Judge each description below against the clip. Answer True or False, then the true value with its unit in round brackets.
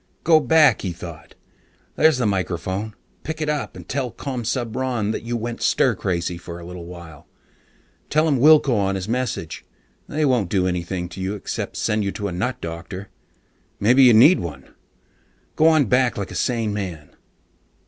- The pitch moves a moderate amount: False (6.2 semitones)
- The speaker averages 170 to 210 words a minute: True (175 wpm)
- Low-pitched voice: True (105 Hz)